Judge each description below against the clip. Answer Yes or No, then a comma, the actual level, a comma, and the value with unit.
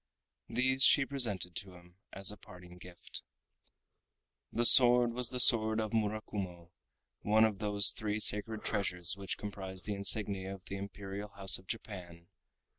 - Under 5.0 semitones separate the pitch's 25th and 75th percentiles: Yes, narrow, 2.6 semitones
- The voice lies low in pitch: Yes, low, 100 Hz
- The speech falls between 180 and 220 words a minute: No, average, 150 wpm